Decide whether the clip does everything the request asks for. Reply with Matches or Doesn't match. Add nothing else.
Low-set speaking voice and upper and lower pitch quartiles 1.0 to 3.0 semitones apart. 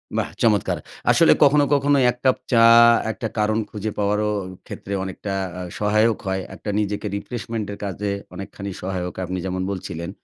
Matches